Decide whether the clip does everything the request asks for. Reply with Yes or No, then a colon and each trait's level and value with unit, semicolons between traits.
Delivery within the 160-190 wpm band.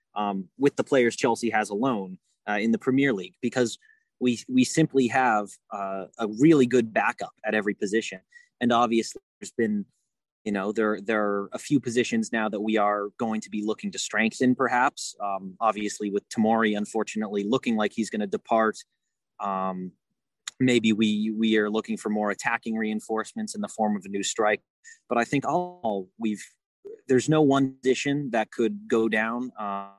Yes: average, 180 wpm